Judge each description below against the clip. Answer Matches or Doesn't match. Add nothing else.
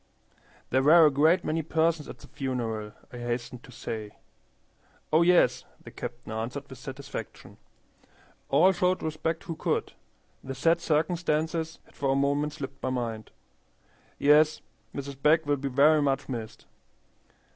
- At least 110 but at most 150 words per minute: Matches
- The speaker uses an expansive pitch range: Doesn't match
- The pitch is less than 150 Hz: Matches